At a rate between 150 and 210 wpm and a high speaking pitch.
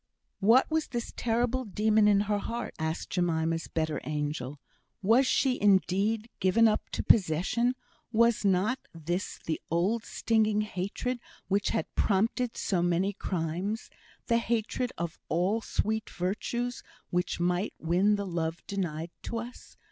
No: average, 140 wpm; high, 200 Hz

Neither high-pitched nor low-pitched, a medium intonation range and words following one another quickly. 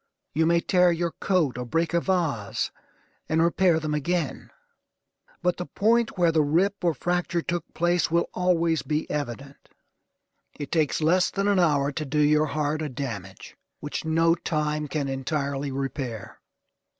No: medium, 160 Hz; average, 3.2 semitones; average, 160 wpm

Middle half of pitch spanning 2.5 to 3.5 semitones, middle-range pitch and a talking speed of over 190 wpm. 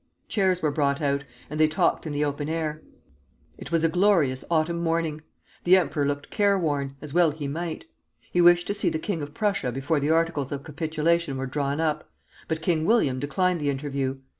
Yes: average, 3.0 semitones; medium, 155 Hz; average, 200 wpm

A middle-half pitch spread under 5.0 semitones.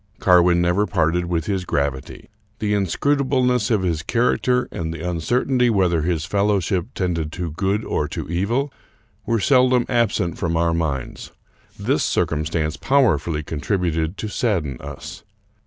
No: average, 5.3 semitones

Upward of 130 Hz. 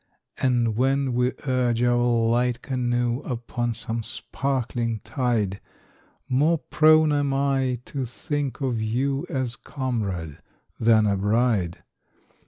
No: low, 120 Hz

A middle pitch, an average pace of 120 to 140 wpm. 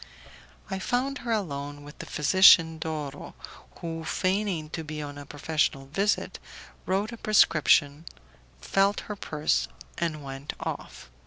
Yes: medium, 160 Hz; slow, 135 wpm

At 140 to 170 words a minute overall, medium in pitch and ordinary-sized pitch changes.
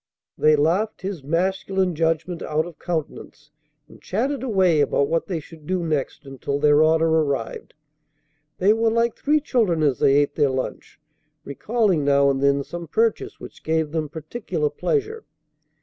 Yes: average, 160 wpm; medium, 160 Hz; average, 4.9 semitones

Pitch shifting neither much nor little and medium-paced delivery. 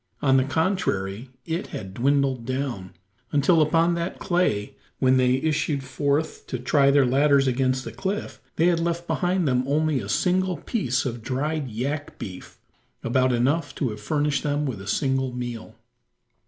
Yes: average, 3.8 semitones; average, 165 wpm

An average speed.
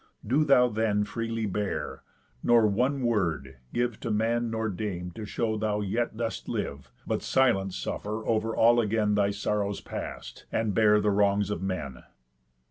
Yes: average, 160 wpm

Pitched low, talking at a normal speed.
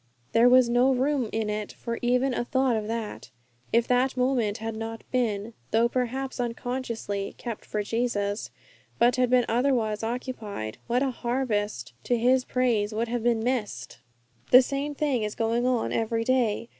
No: high, 235 Hz; average, 170 wpm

